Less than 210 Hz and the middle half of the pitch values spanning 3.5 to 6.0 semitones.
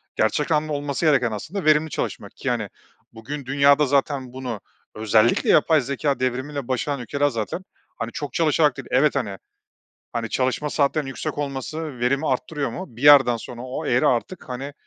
No: medium, 140 Hz; average, 3.1 semitones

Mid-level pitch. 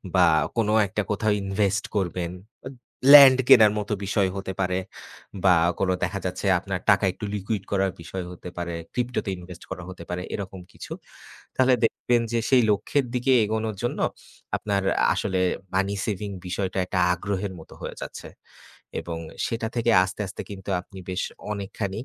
No: low, 100 Hz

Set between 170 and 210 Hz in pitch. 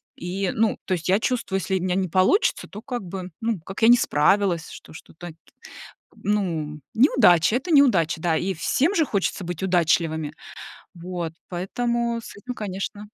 Yes: high, 190 Hz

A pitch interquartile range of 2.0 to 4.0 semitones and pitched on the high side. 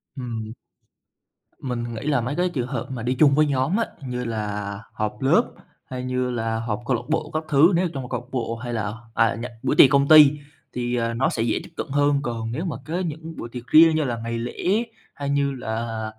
No: average, 3.7 semitones; low, 125 Hz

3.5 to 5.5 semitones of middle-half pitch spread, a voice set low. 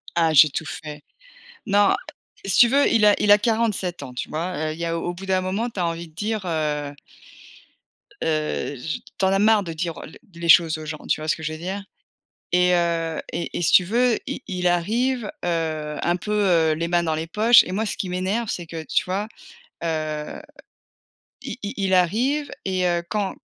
No: average, 4.1 semitones; medium, 175 Hz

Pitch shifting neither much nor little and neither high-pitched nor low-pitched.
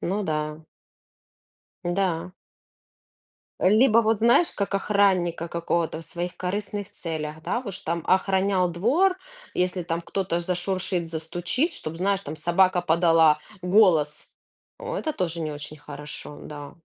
Yes: average, 3.3 semitones; medium, 175 Hz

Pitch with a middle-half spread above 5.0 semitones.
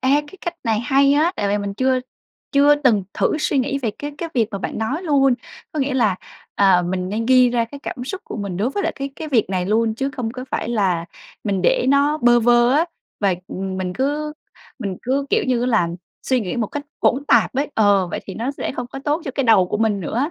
Yes: wide, 5.4 semitones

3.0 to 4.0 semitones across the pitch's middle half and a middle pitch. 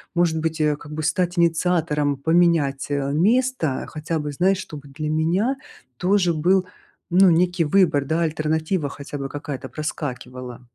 Yes: average, 3.3 semitones; medium, 160 Hz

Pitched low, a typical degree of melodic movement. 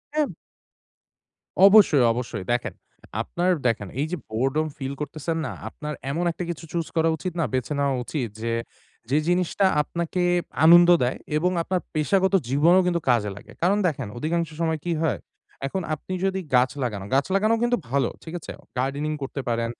No: medium, 155 Hz; average, 4.8 semitones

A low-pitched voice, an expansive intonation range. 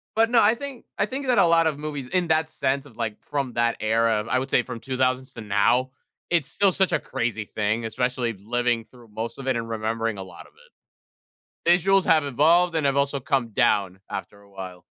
Yes: low, 130 Hz; wide, 5.9 semitones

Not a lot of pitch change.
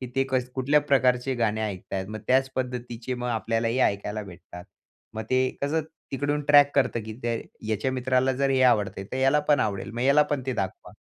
No: average, 3.5 semitones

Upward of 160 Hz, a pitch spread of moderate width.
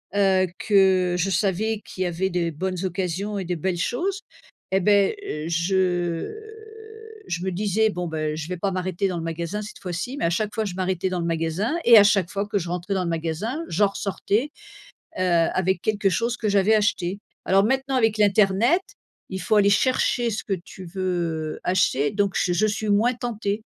Yes: high, 190 Hz; average, 3.0 semitones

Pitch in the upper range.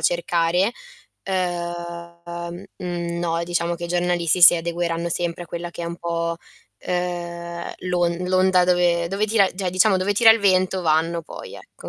No: medium, 175 Hz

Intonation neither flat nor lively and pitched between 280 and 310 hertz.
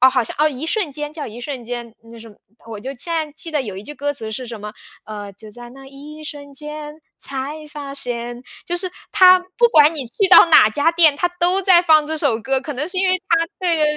Yes: average, 4.8 semitones; very high, 290 Hz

